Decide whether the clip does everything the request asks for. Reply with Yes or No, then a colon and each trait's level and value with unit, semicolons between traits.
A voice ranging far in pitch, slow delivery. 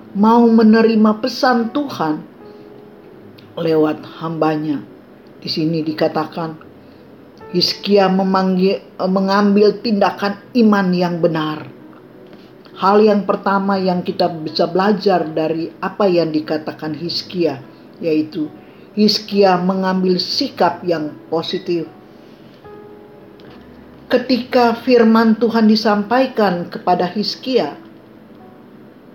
No: average, 4.7 semitones; slow, 80 wpm